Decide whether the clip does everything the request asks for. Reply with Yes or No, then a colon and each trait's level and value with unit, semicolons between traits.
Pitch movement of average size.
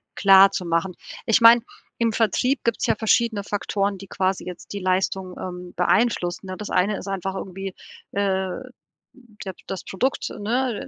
Yes: average, 3.0 semitones